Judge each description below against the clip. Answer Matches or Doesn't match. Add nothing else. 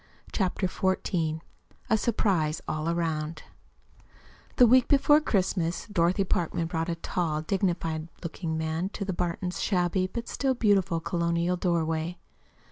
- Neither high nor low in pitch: Matches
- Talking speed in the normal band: Doesn't match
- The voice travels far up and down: Doesn't match